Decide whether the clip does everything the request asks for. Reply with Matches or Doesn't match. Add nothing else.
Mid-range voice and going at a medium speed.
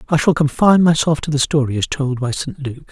Doesn't match